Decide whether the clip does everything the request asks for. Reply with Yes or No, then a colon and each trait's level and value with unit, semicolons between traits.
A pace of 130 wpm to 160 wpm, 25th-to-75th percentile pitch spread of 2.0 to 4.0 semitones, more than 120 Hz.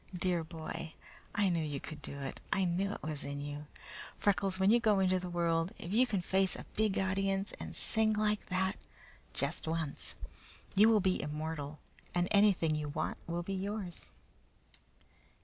No: average, 175 wpm; average, 3.7 semitones; medium, 185 Hz